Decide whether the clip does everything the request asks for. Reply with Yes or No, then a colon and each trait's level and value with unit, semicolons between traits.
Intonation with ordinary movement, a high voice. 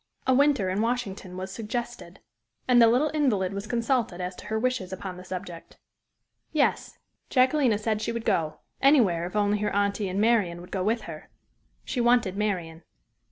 Yes: average, 4.5 semitones; high, 210 Hz